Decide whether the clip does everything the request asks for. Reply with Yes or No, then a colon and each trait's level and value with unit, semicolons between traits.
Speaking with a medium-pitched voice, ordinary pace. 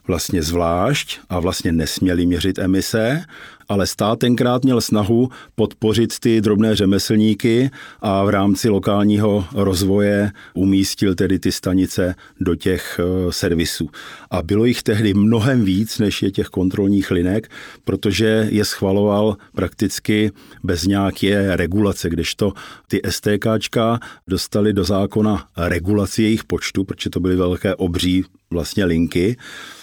No: low, 100 Hz; average, 125 wpm